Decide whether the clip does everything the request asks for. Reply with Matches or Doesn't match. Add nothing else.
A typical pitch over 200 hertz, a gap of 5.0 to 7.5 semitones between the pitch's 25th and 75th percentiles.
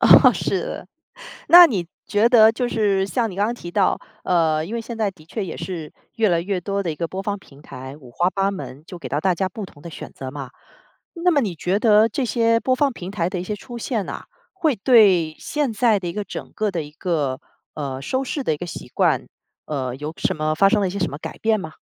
Doesn't match